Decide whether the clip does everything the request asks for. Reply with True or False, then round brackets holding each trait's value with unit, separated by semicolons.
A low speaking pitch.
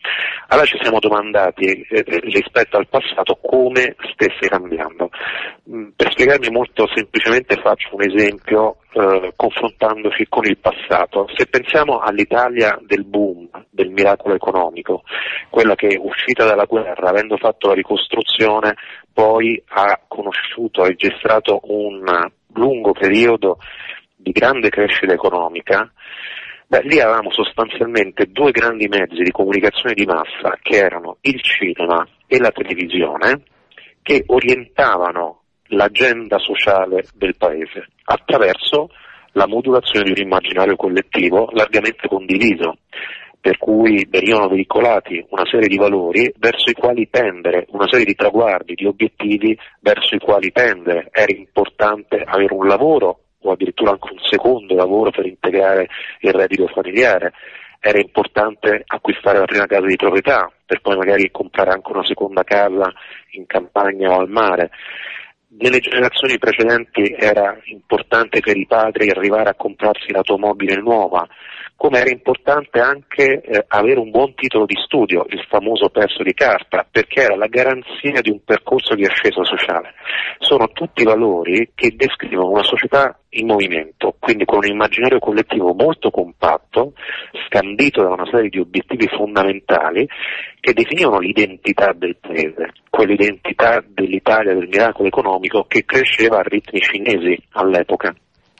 True (105 Hz)